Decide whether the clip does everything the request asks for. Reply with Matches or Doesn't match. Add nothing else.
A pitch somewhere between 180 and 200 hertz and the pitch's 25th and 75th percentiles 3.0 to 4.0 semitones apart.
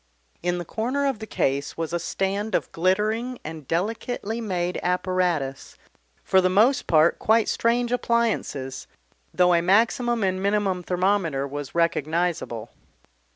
Doesn't match